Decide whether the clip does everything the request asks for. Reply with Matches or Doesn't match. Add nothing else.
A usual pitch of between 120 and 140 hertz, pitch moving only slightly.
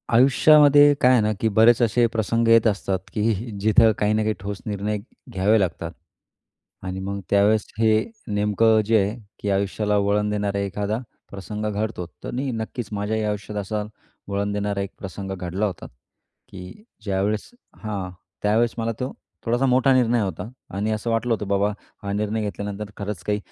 Doesn't match